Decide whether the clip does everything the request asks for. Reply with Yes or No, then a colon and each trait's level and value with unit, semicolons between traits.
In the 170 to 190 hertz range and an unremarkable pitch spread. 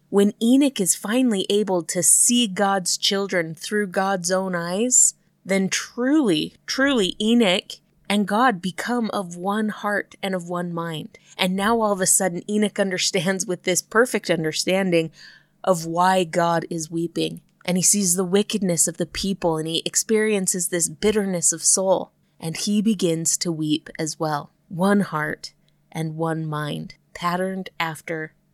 Yes: medium, 185 Hz; average, 3.5 semitones